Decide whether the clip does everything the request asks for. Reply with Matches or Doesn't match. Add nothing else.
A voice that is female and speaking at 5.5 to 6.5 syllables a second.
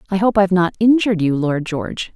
Matches